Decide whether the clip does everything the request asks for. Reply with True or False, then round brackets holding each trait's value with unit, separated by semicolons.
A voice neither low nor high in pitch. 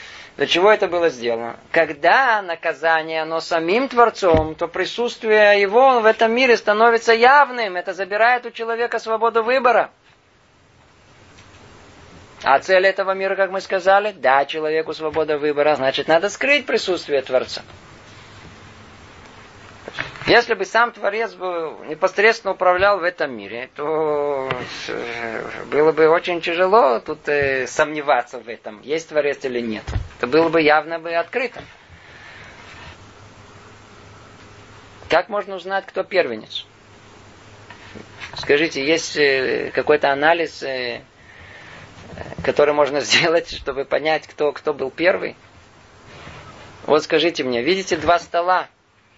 True (155 Hz)